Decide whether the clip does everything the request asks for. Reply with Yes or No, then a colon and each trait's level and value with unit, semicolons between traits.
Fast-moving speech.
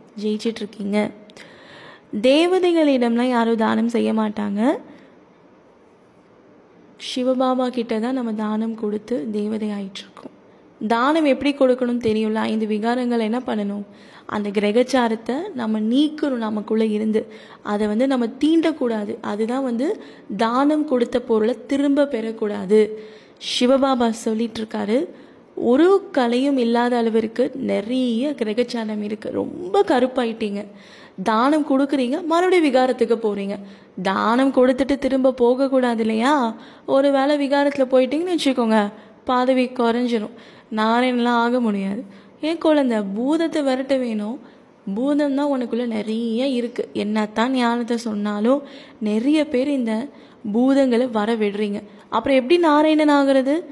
No: average, 105 wpm